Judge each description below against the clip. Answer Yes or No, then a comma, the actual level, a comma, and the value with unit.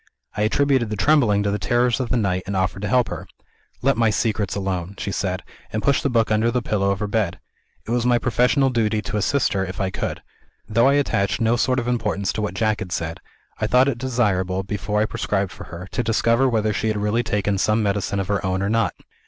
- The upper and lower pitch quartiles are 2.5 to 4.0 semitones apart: Yes, average, 3.4 semitones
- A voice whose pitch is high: No, low, 105 Hz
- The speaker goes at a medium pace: No, fast, 240 wpm